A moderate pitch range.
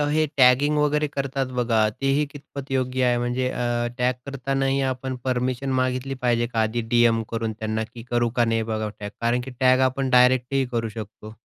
No: narrow, 2.3 semitones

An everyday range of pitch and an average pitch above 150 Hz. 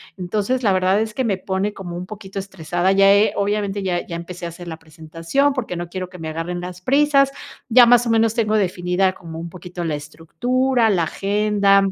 Yes: average, 3.6 semitones; high, 190 Hz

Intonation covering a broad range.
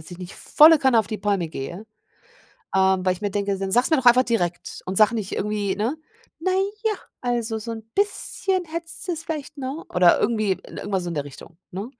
Yes: wide, 7.2 semitones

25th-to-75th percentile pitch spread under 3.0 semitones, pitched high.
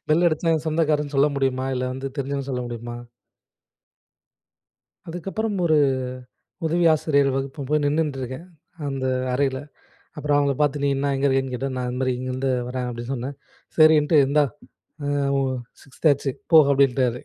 No: narrow, 2.6 semitones; medium, 140 Hz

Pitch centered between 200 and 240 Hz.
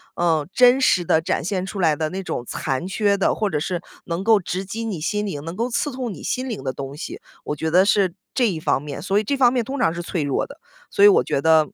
No: high, 190 Hz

